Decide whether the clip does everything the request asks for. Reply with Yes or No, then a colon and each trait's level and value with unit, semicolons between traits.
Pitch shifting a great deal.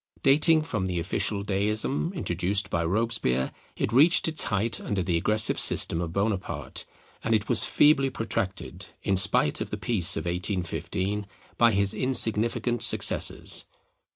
No: average, 3.9 semitones